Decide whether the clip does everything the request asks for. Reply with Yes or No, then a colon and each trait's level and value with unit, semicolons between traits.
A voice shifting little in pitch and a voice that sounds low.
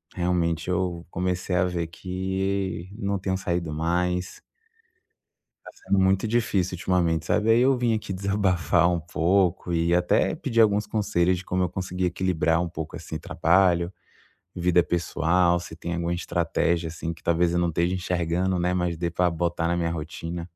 Yes: narrow, 1.7 semitones; very low, 90 Hz